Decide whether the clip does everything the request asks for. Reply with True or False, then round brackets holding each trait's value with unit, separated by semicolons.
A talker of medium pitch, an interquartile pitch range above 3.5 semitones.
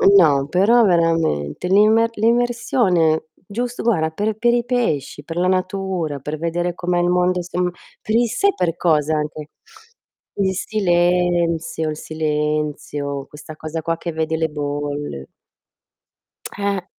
True (175 Hz; 4.4 semitones)